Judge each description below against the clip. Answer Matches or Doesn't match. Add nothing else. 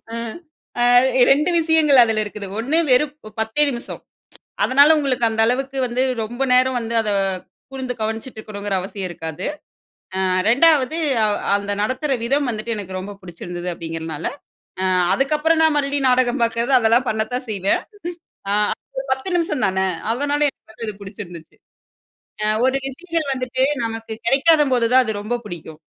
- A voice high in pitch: Matches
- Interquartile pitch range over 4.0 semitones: Matches